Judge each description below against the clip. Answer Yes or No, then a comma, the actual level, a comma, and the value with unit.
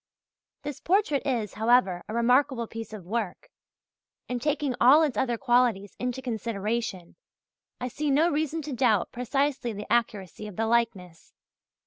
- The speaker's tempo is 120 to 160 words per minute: Yes, average, 145 wpm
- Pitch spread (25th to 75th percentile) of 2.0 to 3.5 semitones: No, average, 4.1 semitones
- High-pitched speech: Yes, high, 235 Hz